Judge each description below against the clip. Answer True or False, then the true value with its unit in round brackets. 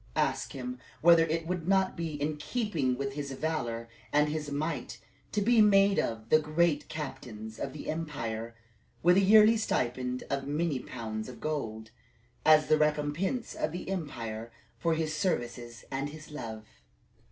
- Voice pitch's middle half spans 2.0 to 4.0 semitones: False (5.1 semitones)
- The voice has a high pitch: False (150 Hz)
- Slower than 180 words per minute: True (165 wpm)